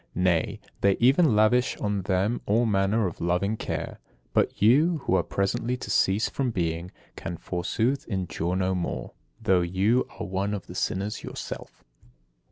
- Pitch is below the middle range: Yes, low, 100 Hz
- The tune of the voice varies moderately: Yes, average, 3.8 semitones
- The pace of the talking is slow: No, average, 160 wpm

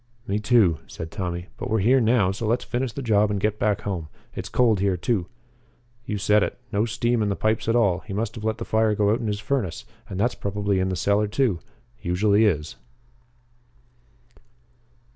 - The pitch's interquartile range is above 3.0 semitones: No, narrow, 2.5 semitones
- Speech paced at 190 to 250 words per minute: Yes, average, 200 wpm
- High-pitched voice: No, low, 105 Hz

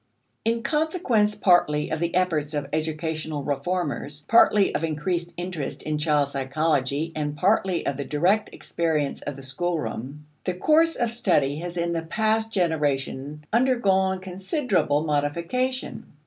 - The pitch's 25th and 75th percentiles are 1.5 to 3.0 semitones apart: No, average, 4.6 semitones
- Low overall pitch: No, medium, 165 Hz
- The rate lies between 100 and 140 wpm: Yes, slow, 135 wpm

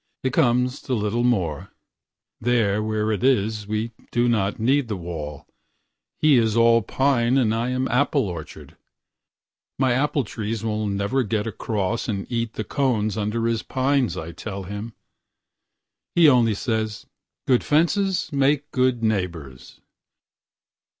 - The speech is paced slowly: Yes, slow, 125 wpm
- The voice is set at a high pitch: No, low, 115 Hz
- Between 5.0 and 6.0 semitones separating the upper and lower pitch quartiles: No, average, 3.7 semitones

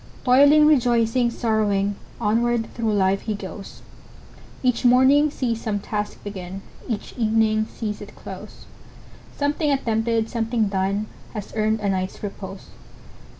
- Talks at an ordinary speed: No, slow, 115 wpm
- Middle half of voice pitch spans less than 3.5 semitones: Yes, average, 2.9 semitones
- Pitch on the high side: Yes, high, 220 Hz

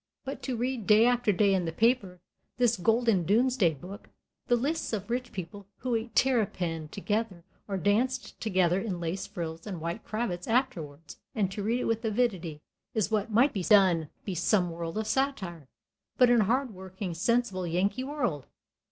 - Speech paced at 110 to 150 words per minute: No, average, 180 wpm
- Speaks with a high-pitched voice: Yes, high, 205 Hz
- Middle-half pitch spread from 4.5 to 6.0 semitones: Yes, average, 5.1 semitones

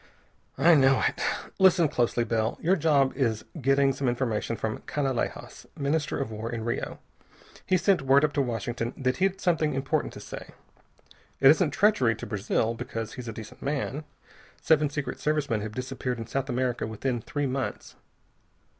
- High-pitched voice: No, low, 135 Hz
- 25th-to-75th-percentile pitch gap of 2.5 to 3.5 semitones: No, average, 4.1 semitones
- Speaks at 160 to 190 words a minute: Yes, average, 170 wpm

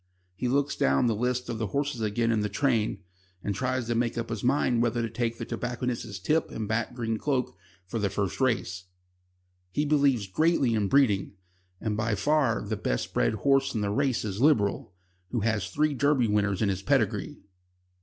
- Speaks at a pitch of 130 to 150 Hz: No, low, 115 Hz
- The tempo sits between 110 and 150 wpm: No, average, 195 wpm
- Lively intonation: No, average, 3.8 semitones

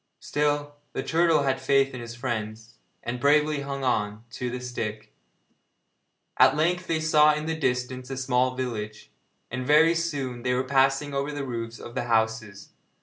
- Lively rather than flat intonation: No, average, 3.5 semitones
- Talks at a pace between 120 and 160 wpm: No, average, 170 wpm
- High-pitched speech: No, low, 130 Hz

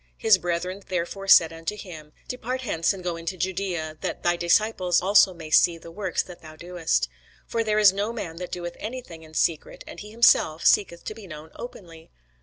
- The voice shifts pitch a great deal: No, average, 3.7 semitones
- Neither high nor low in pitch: Yes, medium, 180 Hz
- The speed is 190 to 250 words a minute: Yes, fast, 205 wpm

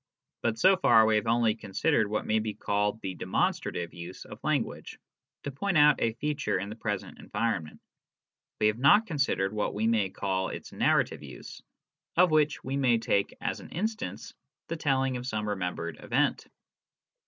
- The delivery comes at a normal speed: Yes, average, 190 wpm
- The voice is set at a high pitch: No, low, 115 Hz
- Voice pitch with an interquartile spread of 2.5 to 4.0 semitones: No, wide, 5.6 semitones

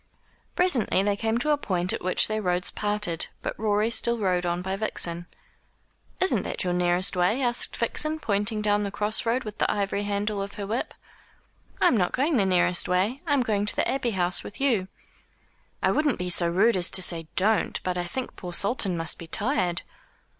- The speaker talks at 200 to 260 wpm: Yes, fast, 205 wpm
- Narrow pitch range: No, average, 4.2 semitones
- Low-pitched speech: No, high, 205 Hz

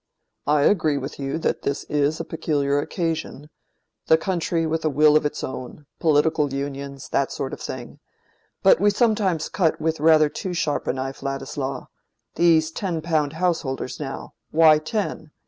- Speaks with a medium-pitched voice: Yes, medium, 155 Hz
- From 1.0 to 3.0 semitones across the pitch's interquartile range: Yes, narrow, 2.5 semitones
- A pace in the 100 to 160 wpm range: Yes, average, 145 wpm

